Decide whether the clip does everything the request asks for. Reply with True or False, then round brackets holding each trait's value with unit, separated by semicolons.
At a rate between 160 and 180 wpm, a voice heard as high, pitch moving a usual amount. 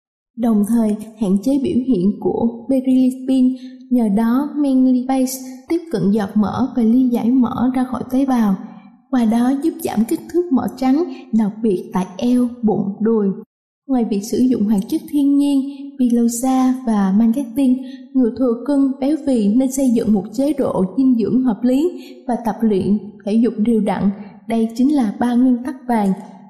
True (175 wpm; 245 Hz; 3.4 semitones)